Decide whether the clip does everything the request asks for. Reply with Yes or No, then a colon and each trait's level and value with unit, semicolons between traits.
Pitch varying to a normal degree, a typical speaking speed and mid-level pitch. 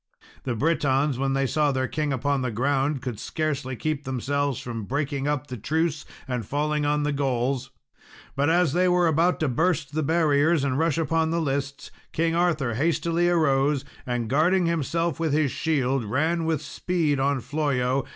Yes: average, 3.2 semitones; average, 175 wpm; medium, 145 Hz